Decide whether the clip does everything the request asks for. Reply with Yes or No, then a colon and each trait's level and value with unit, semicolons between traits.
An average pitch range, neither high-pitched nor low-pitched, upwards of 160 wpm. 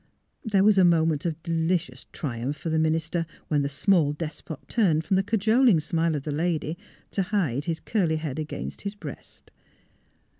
Yes: average, 3.7 semitones; medium, 165 Hz; average, 175 wpm